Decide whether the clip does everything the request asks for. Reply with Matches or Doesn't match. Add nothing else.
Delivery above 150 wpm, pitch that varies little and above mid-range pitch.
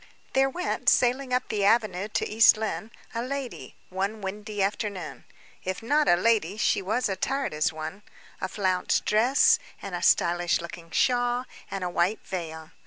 Doesn't match